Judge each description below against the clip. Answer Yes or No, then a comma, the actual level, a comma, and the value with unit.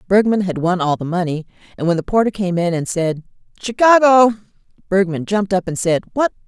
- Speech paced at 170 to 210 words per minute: Yes, average, 195 wpm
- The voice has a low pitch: No, high, 190 Hz